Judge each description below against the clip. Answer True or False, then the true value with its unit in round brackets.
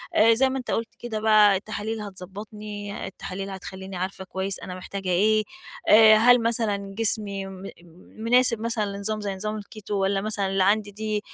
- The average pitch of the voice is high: True (210 Hz)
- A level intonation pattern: True (1.9 semitones)